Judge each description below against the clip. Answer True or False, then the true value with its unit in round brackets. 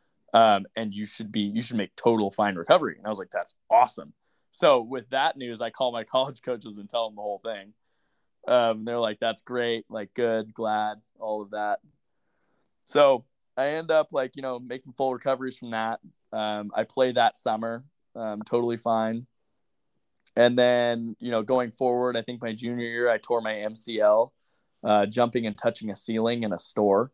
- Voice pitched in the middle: False (115 Hz)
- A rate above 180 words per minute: True (190 wpm)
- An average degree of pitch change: False (2.3 semitones)